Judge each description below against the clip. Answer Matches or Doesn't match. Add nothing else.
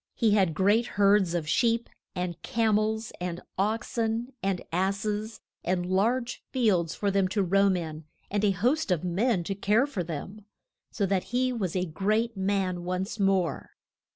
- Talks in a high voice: Matches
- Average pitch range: Matches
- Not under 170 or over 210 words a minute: Matches